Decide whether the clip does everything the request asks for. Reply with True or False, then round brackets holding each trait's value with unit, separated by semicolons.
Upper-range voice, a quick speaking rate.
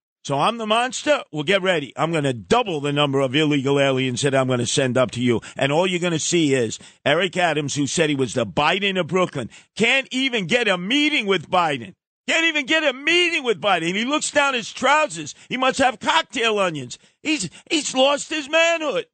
True (195 Hz; 220 wpm)